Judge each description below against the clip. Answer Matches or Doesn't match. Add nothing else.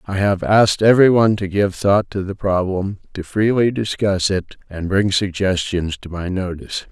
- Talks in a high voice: Doesn't match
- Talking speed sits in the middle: Matches